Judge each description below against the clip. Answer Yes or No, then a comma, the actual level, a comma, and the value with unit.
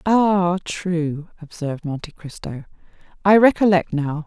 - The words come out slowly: Yes, slow, 115 wpm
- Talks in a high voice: No, medium, 170 Hz